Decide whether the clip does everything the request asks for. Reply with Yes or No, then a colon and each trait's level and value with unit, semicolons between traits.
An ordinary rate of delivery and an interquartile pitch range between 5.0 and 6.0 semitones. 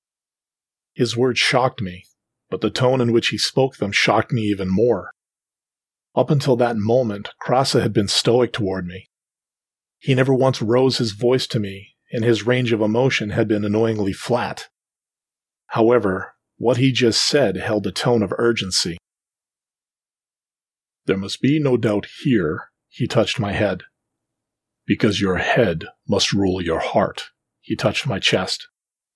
No: average, 150 wpm; average, 3.7 semitones